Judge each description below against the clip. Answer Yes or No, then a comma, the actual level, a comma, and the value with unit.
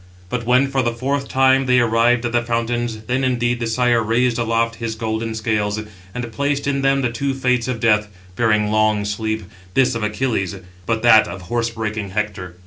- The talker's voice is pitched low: Yes, low, 115 Hz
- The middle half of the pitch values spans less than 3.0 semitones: Yes, narrow, 2.4 semitones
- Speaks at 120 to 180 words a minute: No, average, 195 wpm